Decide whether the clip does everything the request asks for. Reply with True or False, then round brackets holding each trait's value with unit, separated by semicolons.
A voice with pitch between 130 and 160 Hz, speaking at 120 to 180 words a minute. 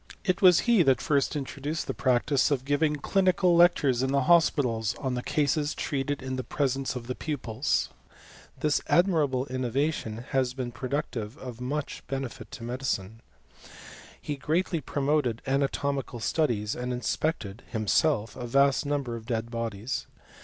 True (135 Hz; 145 wpm)